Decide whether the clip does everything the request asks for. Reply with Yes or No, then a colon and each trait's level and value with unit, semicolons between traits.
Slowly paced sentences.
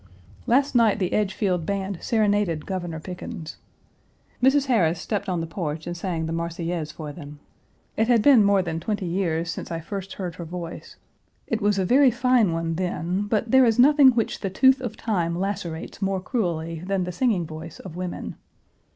No: average, 185 wpm